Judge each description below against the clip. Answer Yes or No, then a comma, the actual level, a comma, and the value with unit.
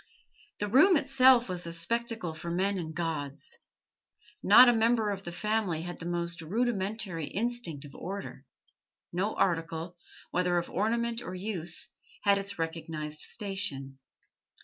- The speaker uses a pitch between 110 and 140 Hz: No, medium, 185 Hz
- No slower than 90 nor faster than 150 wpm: Yes, average, 140 wpm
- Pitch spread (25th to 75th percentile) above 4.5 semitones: Yes, average, 5.1 semitones